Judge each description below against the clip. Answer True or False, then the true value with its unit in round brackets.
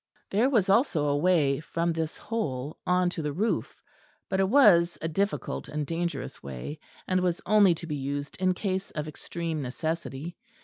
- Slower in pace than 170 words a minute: False (175 wpm)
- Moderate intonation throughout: True (4.0 semitones)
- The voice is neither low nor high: True (170 Hz)